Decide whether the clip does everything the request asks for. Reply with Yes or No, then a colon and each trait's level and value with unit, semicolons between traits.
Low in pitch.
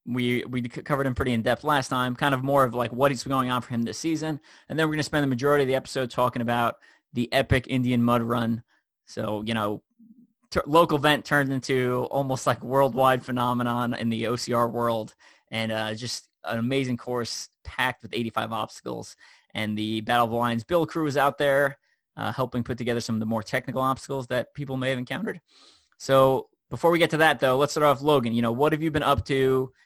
Yes: low, 130 Hz